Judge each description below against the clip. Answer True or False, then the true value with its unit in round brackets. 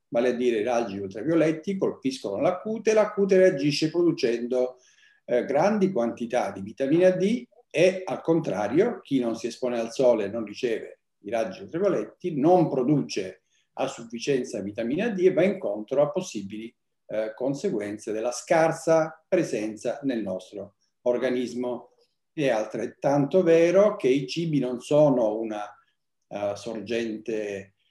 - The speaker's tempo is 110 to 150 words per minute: True (140 wpm)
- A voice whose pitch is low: True (130 Hz)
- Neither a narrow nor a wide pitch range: False (7.8 semitones)